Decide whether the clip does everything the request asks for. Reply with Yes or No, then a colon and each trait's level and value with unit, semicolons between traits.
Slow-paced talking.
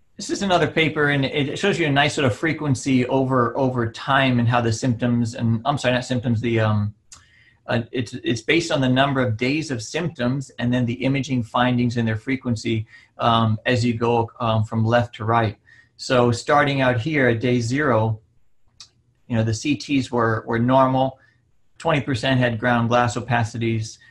No: average, 185 wpm